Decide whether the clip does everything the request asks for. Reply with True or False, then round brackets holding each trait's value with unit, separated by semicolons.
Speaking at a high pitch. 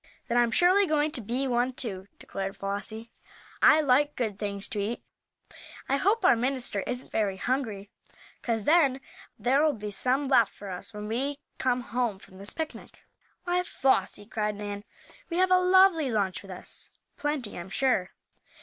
True (245 Hz)